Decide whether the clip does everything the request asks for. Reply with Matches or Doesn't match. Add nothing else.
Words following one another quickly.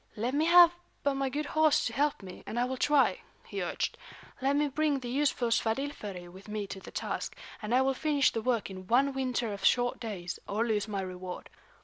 Matches